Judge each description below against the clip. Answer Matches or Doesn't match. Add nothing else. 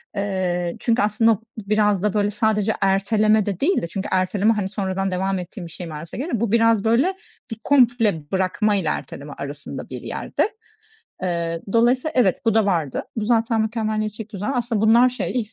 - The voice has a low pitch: Doesn't match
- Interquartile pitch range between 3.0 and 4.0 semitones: Matches